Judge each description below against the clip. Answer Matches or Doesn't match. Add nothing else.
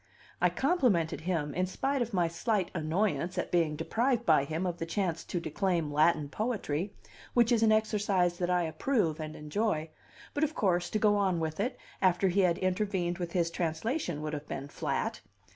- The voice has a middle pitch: Matches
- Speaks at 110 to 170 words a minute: Doesn't match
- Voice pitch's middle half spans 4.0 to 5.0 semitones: Matches